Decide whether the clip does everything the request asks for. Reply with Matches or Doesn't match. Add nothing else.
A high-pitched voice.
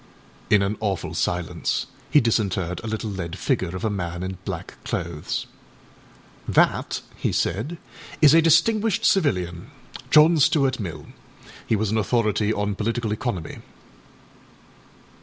Doesn't match